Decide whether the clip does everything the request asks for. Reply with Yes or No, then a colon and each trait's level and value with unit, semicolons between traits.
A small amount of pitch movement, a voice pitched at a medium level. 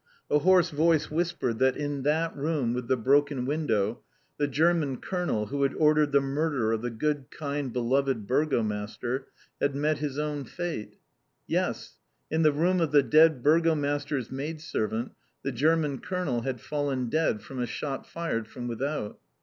No: average, 3.6 semitones; medium, 145 Hz